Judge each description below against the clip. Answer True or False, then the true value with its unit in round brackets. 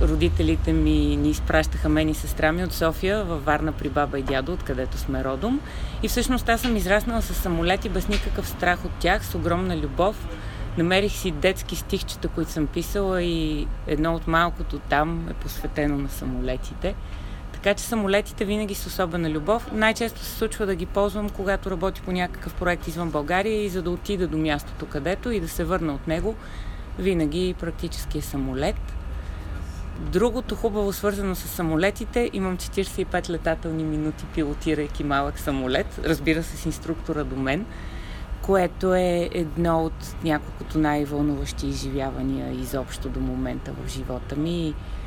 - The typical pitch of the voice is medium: True (165 Hz)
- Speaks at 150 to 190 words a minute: True (155 wpm)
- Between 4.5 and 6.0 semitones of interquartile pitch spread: True (5.3 semitones)